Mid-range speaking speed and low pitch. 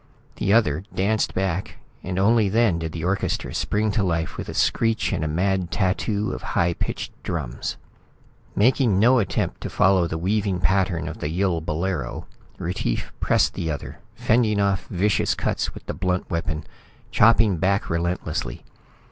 Yes: average, 160 wpm; very low, 95 Hz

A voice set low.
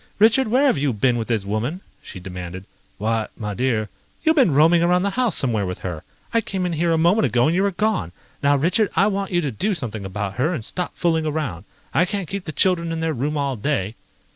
No: medium, 155 Hz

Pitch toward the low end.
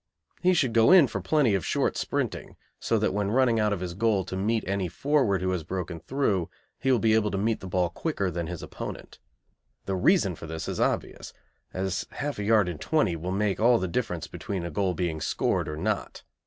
Yes: low, 100 Hz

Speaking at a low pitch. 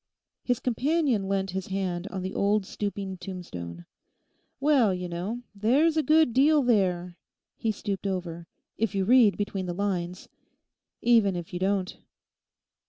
No: high, 195 Hz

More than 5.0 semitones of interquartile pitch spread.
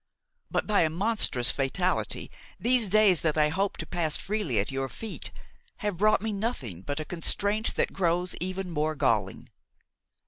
Yes: wide, 5.6 semitones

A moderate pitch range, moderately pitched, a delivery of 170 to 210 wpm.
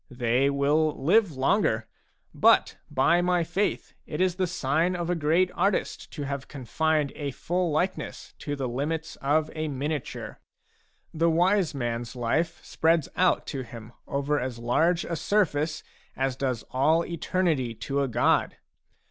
No: average, 4.2 semitones; medium, 150 Hz; average, 150 wpm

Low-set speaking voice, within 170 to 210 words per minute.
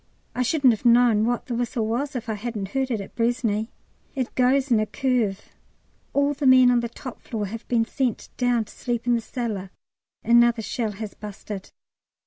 No: high, 235 Hz; average, 195 wpm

